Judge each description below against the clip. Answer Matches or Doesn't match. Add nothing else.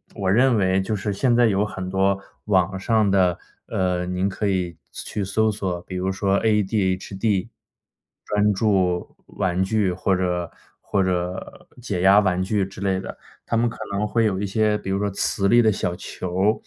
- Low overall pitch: Matches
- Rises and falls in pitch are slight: Matches